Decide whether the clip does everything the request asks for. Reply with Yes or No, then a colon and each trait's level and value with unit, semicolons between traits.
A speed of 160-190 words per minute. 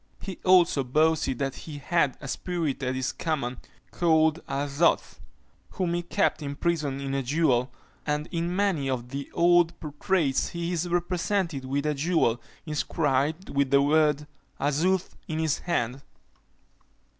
No: average, 145 wpm